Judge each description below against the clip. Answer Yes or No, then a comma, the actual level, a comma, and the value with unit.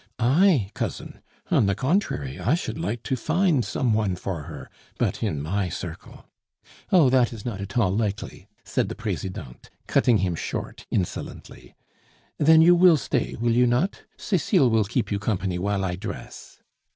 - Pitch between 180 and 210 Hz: No, low, 110 Hz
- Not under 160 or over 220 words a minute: Yes, average, 170 wpm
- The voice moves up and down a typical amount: No, wide, 6.2 semitones